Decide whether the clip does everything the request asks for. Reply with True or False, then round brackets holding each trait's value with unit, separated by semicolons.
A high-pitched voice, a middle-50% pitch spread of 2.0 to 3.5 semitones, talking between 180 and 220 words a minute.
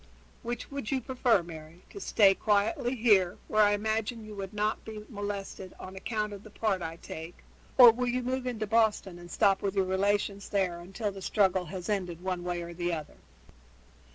True (205 Hz; 3.1 semitones; 195 wpm)